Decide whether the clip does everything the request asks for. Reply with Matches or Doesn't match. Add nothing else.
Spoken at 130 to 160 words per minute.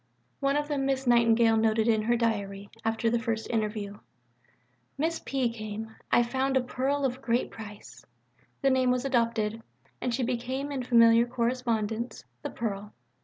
Doesn't match